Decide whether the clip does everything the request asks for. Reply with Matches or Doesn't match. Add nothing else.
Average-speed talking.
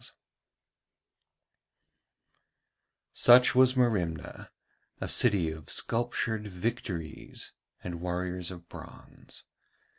Doesn't match